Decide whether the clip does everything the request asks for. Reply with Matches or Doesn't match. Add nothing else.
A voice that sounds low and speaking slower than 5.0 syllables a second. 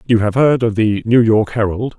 Doesn't match